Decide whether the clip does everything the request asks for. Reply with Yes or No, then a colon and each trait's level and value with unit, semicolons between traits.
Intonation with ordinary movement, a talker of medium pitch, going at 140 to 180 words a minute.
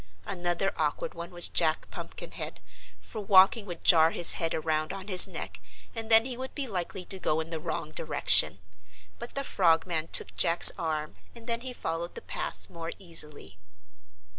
Yes: average, 3.6 semitones; medium, 175 Hz; average, 175 wpm